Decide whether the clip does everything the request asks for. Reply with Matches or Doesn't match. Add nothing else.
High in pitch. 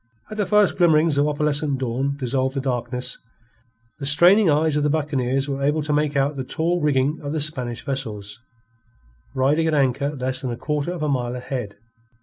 Doesn't match